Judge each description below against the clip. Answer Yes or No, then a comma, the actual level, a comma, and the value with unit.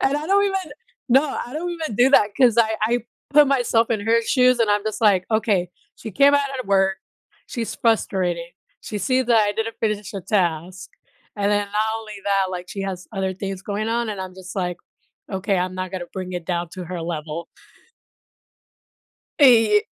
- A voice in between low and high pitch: No, high, 210 Hz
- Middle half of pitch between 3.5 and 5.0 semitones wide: Yes, average, 4.1 semitones